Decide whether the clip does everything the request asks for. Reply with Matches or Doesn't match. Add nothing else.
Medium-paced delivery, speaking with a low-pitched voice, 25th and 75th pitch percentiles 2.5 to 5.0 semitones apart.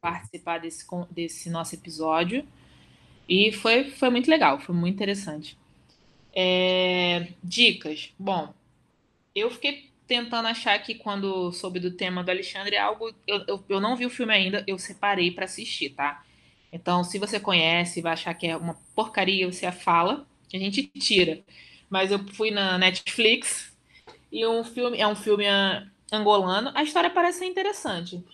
Doesn't match